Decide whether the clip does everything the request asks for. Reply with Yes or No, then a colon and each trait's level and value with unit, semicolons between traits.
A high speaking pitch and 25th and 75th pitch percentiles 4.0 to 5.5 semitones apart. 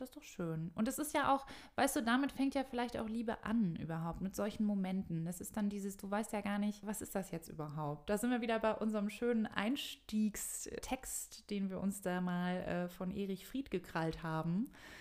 Yes: high, 210 Hz; average, 4.5 semitones